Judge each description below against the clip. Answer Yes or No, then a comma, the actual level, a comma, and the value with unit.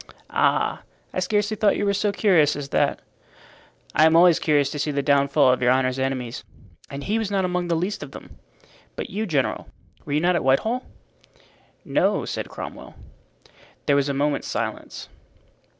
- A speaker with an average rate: Yes, average, 180 wpm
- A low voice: No, medium, 155 Hz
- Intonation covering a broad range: Yes, wide, 5.7 semitones